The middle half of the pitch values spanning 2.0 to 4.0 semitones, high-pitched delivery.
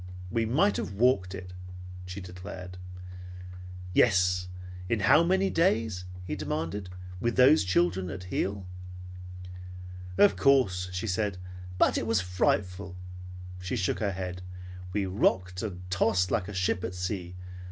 No: average, 3.1 semitones; very low, 95 Hz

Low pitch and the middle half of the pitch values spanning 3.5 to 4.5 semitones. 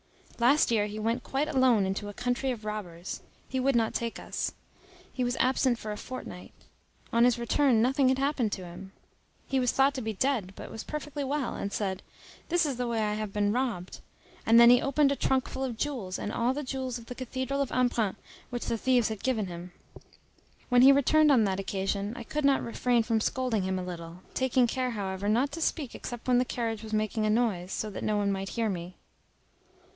No: high, 235 Hz; average, 3.9 semitones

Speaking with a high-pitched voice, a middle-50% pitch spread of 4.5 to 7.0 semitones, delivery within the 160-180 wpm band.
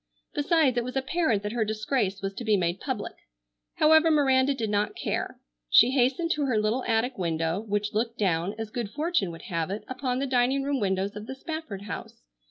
No: high, 230 Hz; average, 4.8 semitones; average, 200 wpm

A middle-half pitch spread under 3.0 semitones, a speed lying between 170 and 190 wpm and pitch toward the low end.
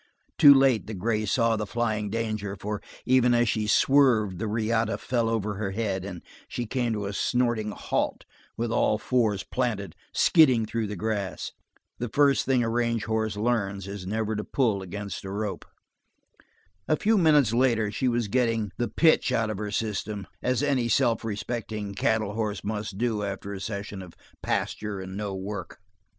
Yes: narrow, 2.6 semitones; average, 175 wpm; low, 110 Hz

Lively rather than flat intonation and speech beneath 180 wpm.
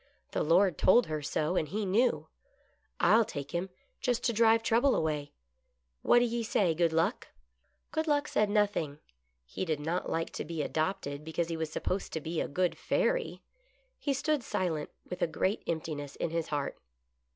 No: wide, 6.2 semitones; average, 185 wpm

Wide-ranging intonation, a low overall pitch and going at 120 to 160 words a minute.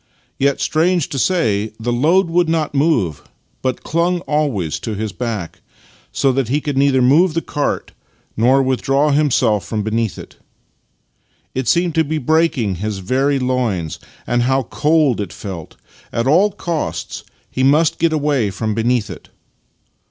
Yes: wide, 5.8 semitones; low, 130 Hz; average, 155 wpm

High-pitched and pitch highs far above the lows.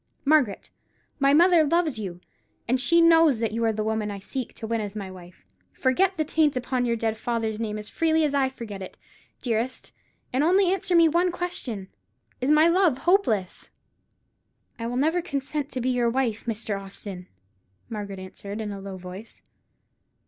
Yes: high, 245 Hz; wide, 6.6 semitones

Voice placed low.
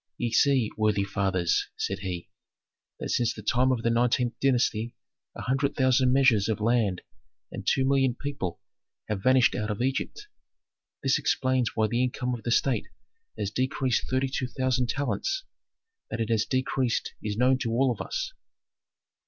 Yes: low, 125 Hz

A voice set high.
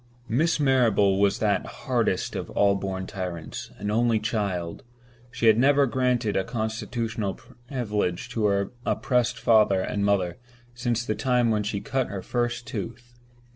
No: low, 110 Hz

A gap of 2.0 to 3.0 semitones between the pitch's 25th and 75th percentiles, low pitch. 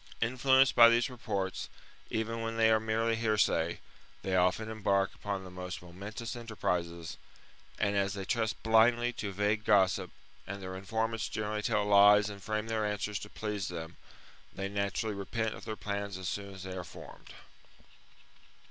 Yes: narrow, 2.5 semitones; low, 105 Hz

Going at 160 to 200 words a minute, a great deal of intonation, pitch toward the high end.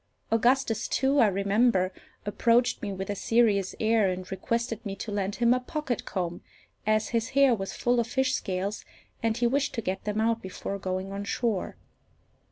No: average, 180 wpm; average, 3.5 semitones; high, 220 Hz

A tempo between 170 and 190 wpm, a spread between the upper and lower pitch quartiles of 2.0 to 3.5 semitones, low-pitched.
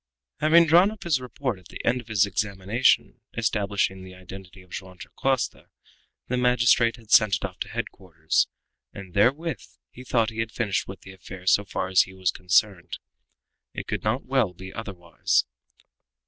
No: average, 175 wpm; average, 4.7 semitones; low, 105 Hz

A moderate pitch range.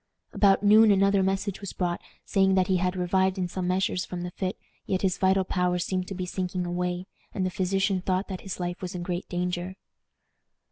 No: narrow, 1.3 semitones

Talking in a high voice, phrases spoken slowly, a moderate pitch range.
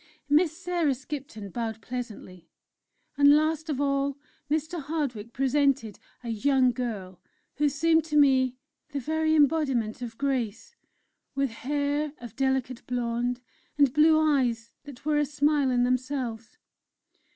Yes: very high, 275 Hz; slow, 130 wpm; average, 3.6 semitones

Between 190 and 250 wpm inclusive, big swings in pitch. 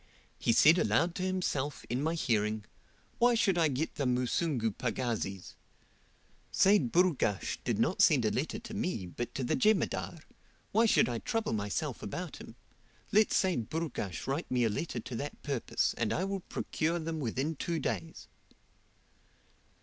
No: average, 160 wpm; wide, 6.9 semitones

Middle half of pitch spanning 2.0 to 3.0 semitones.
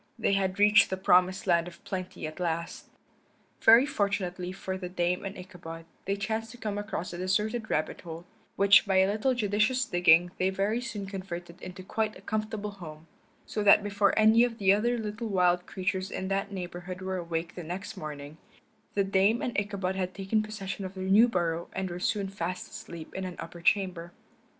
Yes: average, 2.7 semitones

